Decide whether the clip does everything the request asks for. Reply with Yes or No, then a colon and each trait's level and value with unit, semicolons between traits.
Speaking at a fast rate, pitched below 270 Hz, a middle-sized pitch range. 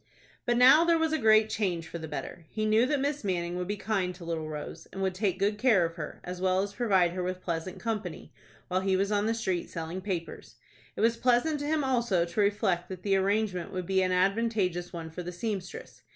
Yes: fast, 235 wpm; high, 190 Hz; average, 3.7 semitones